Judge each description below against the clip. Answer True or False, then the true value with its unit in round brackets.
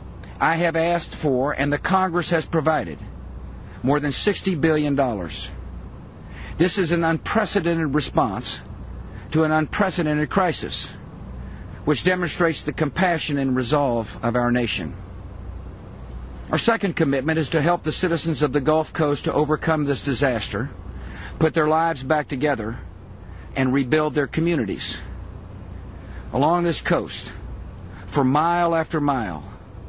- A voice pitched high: False (140 Hz)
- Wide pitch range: True (8.9 semitones)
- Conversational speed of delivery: False (125 wpm)